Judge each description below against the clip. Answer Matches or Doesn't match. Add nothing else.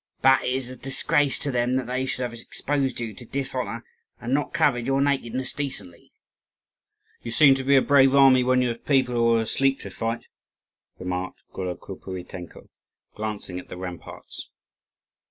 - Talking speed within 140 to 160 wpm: Doesn't match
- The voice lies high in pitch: Doesn't match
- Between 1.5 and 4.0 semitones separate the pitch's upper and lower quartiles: Matches